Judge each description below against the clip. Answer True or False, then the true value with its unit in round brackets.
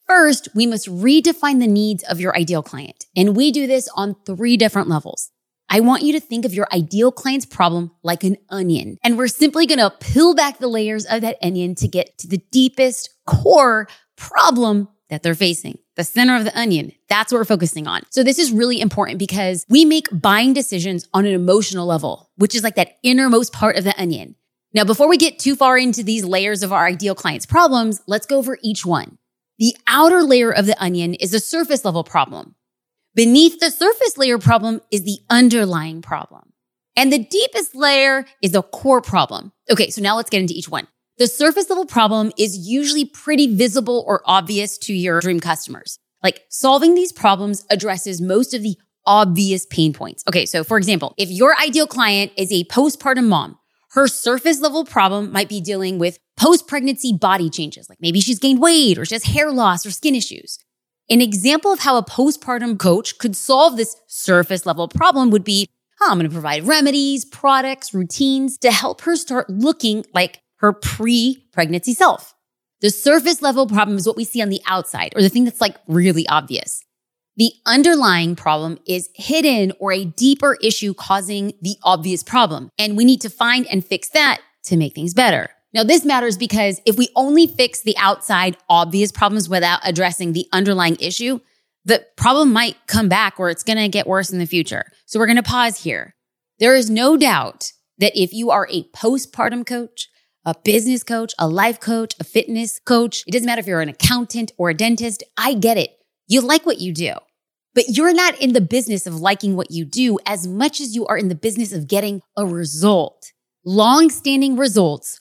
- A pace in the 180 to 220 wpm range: True (195 wpm)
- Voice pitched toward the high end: True (215 Hz)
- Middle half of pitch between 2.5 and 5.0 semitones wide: False (5.6 semitones)